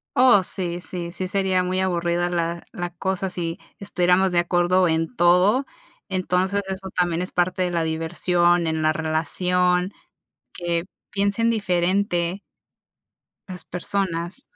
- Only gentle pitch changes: Yes, narrow, 1.7 semitones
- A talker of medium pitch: Yes, medium, 180 Hz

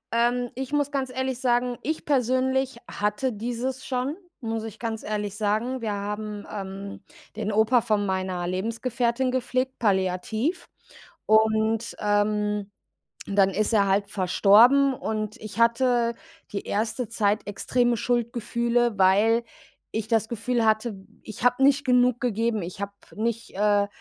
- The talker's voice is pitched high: Yes, high, 225 Hz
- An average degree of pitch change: Yes, average, 3.1 semitones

